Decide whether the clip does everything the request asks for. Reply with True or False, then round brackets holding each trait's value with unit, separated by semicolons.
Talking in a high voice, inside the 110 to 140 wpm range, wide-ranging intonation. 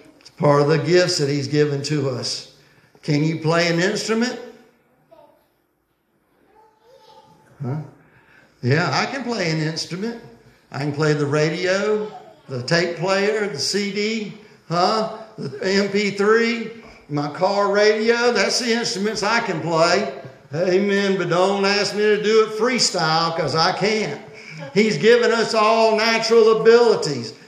True (195 Hz; 135 wpm; 6.1 semitones)